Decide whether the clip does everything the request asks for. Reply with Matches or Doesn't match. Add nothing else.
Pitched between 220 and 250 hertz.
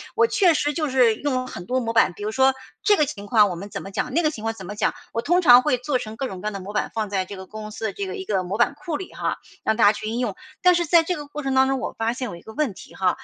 Matches